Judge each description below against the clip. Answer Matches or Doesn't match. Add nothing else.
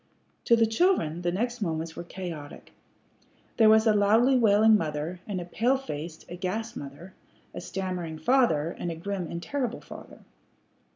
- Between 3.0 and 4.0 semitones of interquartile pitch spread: Doesn't match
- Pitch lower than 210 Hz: Matches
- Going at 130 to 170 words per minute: Matches